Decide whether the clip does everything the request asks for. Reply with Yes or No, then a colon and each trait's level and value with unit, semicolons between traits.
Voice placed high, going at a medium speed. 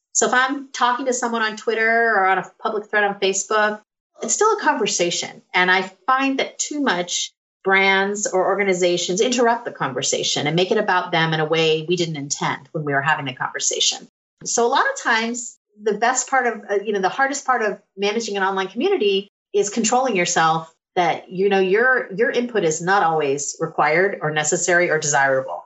Yes: high, 200 Hz; average, 195 wpm